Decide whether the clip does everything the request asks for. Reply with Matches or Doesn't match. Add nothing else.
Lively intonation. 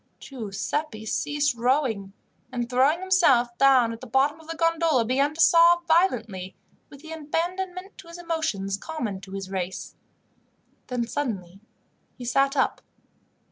Matches